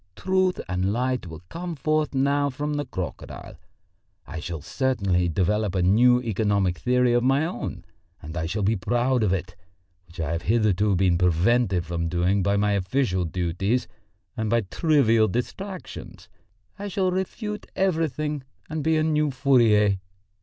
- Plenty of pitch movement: Yes, wide, 7.6 semitones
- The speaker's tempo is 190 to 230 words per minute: No, average, 155 wpm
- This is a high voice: No, low, 110 Hz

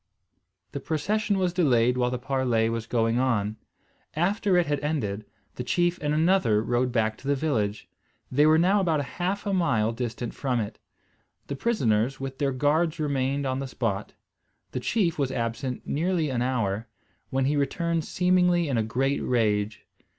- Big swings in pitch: Yes, wide, 5.8 semitones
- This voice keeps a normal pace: Yes, average, 170 wpm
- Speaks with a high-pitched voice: No, low, 135 Hz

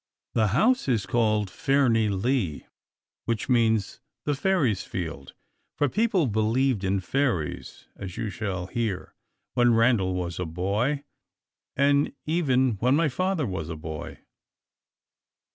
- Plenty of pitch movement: Yes, wide, 6.3 semitones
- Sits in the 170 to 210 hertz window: No, low, 115 Hz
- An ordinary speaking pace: No, slow, 125 wpm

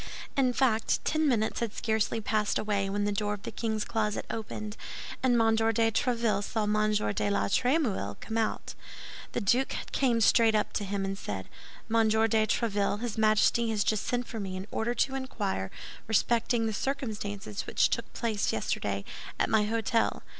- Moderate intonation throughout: No, narrow, 2.0 semitones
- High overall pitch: Yes, high, 220 Hz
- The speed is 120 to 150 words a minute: No, average, 175 wpm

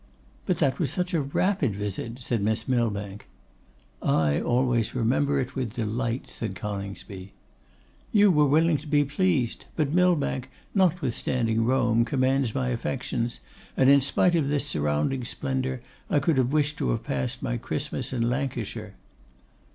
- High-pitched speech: No, low, 130 Hz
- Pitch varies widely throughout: No, average, 4.3 semitones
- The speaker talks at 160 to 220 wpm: No, average, 150 wpm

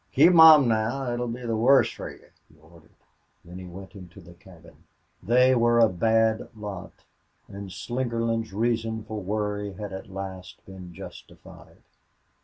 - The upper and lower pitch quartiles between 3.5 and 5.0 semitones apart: Yes, average, 3.9 semitones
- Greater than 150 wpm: Yes, average, 165 wpm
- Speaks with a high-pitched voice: No, low, 105 Hz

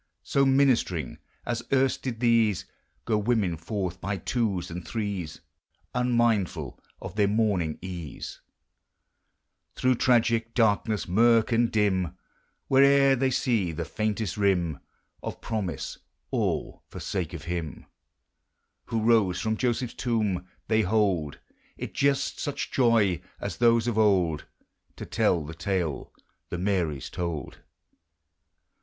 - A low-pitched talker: Yes, low, 105 Hz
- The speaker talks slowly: Yes, slow, 125 wpm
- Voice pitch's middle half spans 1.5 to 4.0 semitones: No, average, 4.9 semitones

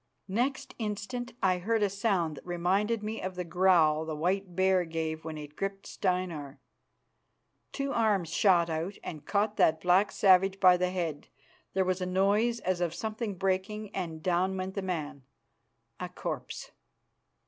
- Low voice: No, medium, 185 Hz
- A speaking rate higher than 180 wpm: No, average, 160 wpm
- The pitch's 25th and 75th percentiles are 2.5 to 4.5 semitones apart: Yes, average, 2.8 semitones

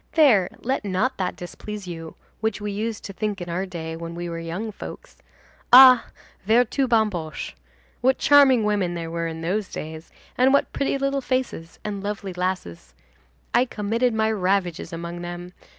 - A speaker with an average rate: Yes, average, 170 wpm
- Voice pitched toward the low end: No, high, 200 Hz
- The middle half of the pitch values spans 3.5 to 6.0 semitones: Yes, average, 5.0 semitones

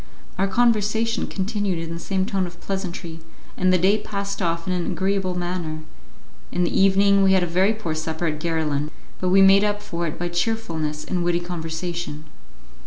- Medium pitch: Yes, medium, 180 Hz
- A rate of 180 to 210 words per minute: Yes, average, 185 wpm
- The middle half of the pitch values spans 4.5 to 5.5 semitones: No, average, 2.8 semitones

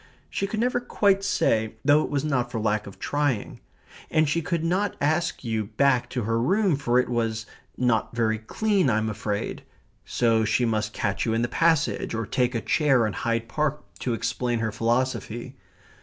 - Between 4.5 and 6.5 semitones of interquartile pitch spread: Yes, average, 5.2 semitones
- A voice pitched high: No, low, 120 Hz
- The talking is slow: No, average, 185 wpm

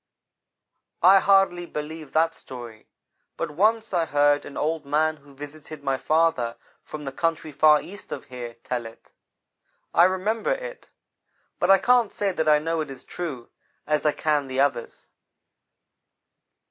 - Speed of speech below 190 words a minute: Yes, average, 155 wpm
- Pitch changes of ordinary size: Yes, average, 3.9 semitones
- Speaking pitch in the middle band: Yes, medium, 155 Hz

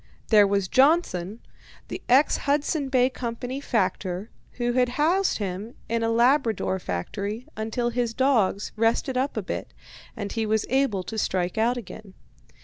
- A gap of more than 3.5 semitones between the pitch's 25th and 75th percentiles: Yes, average, 4.1 semitones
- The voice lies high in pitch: Yes, high, 230 Hz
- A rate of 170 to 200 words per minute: No, average, 150 wpm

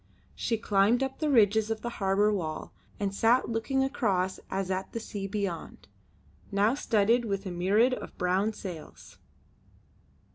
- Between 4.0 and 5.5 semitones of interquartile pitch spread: No, average, 3.1 semitones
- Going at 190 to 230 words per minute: No, average, 150 wpm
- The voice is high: Yes, high, 205 Hz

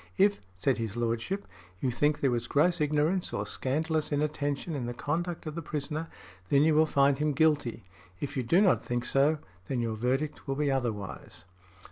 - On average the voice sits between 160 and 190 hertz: No, medium, 145 Hz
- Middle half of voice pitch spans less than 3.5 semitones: No, average, 4.2 semitones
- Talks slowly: No, average, 185 wpm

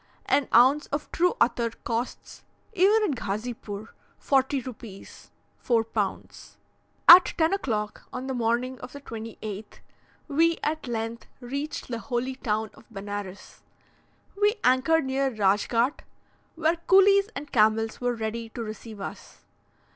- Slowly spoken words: Yes, slow, 130 wpm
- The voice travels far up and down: No, average, 4.6 semitones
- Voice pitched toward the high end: Yes, high, 245 Hz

